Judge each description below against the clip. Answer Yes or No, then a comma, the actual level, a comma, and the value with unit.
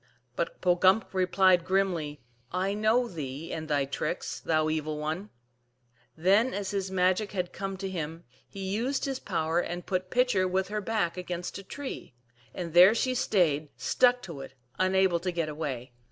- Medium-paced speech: Yes, average, 175 wpm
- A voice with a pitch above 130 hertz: Yes, medium, 185 Hz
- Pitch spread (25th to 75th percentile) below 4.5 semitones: Yes, average, 3.5 semitones